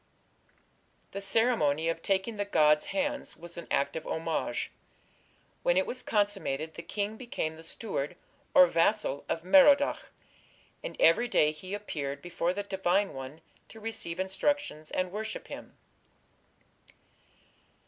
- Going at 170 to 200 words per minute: No, slow, 135 wpm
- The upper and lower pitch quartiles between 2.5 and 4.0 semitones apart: No, average, 5.1 semitones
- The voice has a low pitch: No, medium, 185 Hz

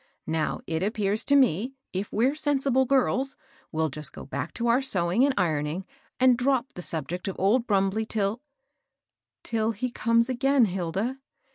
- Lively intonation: Yes, wide, 6.0 semitones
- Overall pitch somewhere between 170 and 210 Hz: No, high, 220 Hz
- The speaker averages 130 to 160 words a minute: No, average, 180 wpm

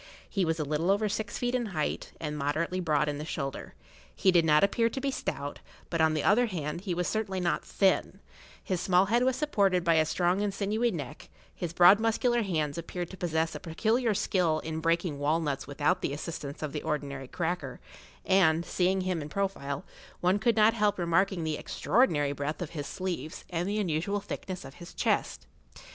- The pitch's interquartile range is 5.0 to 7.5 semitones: No, average, 4.2 semitones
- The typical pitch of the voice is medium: Yes, medium, 175 Hz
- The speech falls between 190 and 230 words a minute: Yes, average, 200 wpm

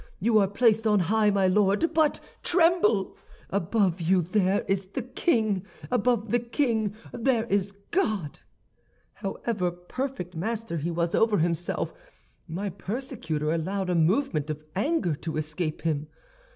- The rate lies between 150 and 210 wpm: No, average, 140 wpm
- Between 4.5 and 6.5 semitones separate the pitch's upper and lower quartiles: Yes, average, 4.8 semitones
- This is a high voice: Yes, high, 200 Hz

